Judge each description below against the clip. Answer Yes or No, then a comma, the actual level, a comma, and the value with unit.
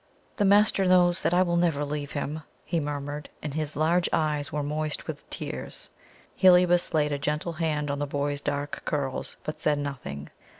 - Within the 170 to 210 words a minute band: Yes, average, 180 wpm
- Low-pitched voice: No, medium, 150 Hz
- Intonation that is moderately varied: Yes, average, 3.0 semitones